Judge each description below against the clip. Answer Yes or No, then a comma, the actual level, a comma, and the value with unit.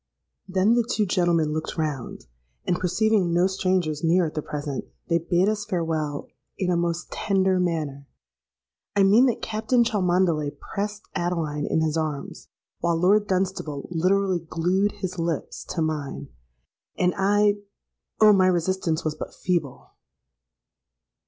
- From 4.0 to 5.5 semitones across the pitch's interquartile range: No, average, 3.6 semitones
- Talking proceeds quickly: No, slow, 135 wpm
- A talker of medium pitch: Yes, medium, 175 Hz